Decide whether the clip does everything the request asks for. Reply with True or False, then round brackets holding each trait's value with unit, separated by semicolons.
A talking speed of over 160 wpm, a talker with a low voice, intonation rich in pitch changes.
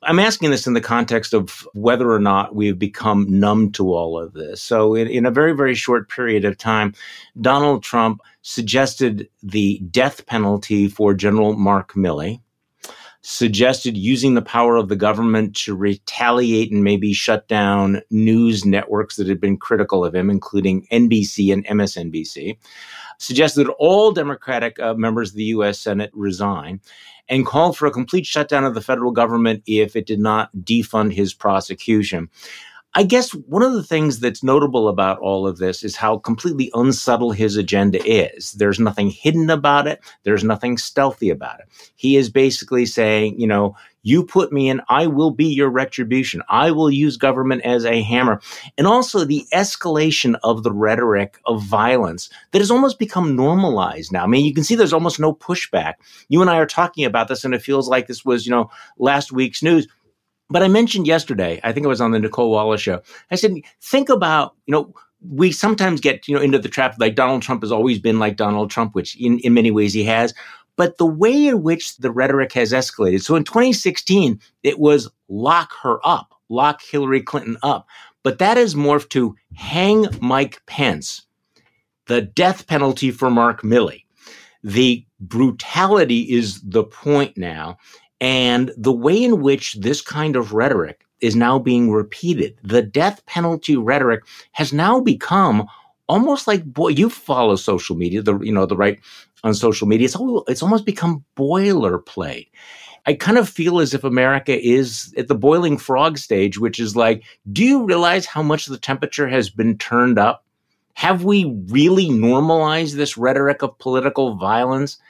True (180 wpm; 125 Hz; 5.7 semitones)